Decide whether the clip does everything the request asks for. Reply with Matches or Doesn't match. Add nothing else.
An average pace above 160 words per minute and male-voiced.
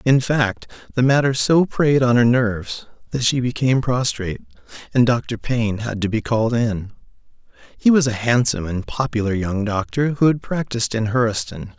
Matches